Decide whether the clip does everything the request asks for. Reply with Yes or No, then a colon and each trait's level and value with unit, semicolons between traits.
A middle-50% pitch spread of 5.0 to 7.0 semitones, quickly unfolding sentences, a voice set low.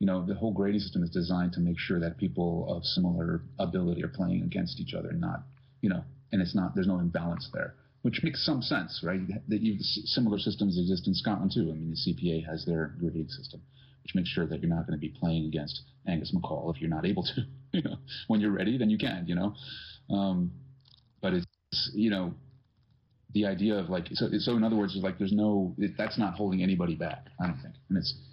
Yes: wide, 5.5 semitones; fast, 235 wpm; low, 100 Hz